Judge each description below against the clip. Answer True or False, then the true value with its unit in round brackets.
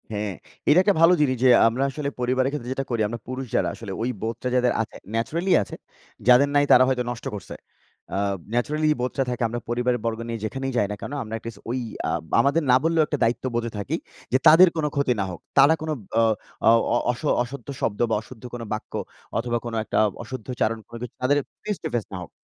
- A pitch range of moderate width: True (3.4 semitones)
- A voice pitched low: True (125 Hz)